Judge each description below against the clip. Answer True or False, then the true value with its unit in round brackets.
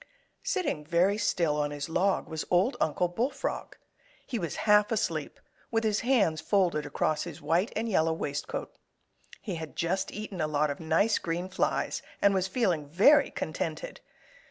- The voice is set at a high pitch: False (180 Hz)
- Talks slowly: False (160 wpm)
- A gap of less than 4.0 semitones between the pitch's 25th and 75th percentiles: False (5.1 semitones)